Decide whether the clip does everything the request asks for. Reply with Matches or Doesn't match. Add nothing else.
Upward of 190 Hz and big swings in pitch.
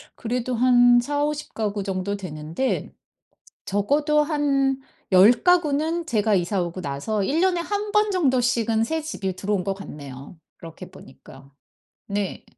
Matches